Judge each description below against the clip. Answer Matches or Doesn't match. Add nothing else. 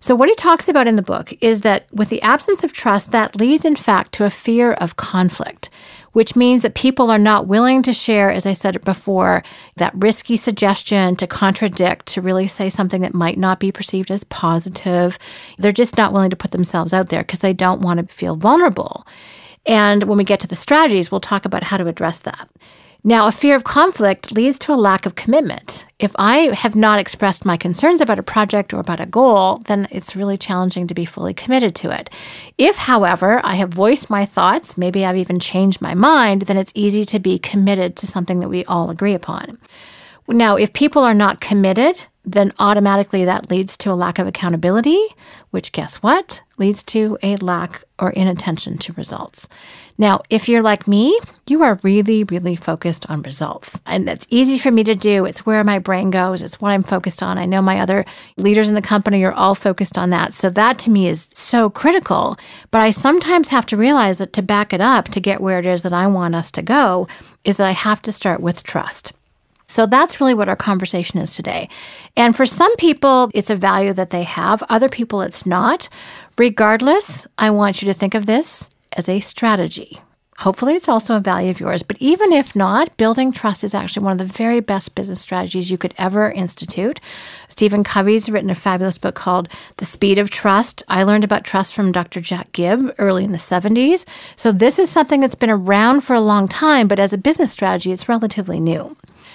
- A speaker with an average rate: Doesn't match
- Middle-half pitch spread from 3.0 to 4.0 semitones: Matches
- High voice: Matches